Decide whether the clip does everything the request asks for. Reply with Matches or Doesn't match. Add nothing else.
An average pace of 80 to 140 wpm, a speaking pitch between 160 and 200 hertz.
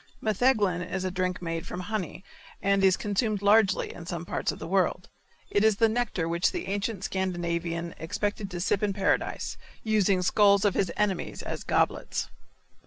Doesn't match